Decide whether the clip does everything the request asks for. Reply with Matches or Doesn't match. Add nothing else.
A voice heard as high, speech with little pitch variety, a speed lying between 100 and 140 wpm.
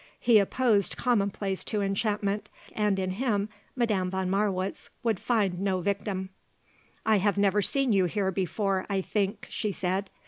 Doesn't match